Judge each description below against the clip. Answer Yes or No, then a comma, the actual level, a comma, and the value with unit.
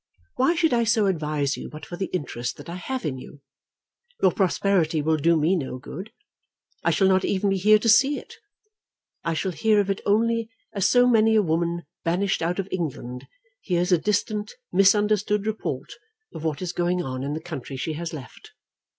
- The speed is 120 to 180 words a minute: No, average, 195 wpm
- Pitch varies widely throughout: No, average, 4.8 semitones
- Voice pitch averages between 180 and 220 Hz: Yes, medium, 185 Hz